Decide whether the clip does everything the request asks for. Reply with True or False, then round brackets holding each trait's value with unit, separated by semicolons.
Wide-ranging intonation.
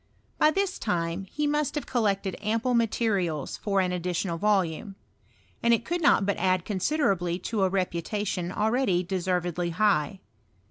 False (4.2 semitones)